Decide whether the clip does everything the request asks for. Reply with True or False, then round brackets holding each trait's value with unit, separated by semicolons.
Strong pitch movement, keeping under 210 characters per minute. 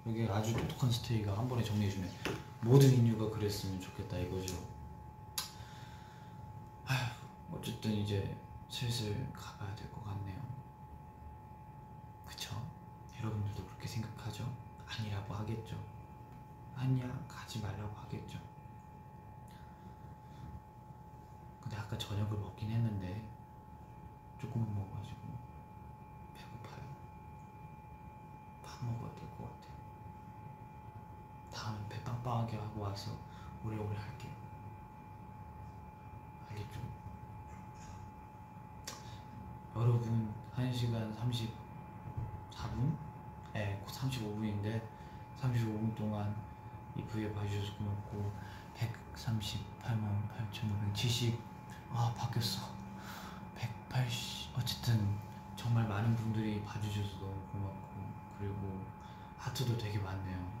False (2.6 semitones; 190 characters per minute)